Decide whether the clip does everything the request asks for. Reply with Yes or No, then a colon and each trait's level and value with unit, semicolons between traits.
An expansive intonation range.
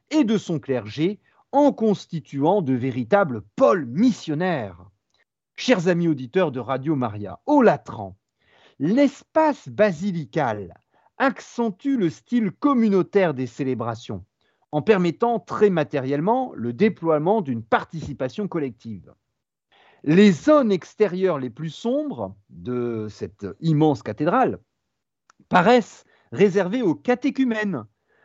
Yes: wide, 9.0 semitones